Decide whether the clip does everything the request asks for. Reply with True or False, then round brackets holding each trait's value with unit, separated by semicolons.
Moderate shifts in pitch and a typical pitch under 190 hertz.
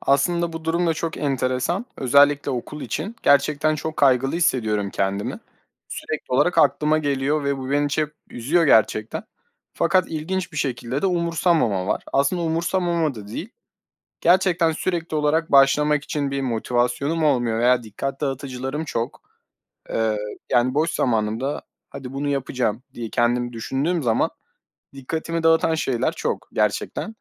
True (4.6 semitones; 140 Hz)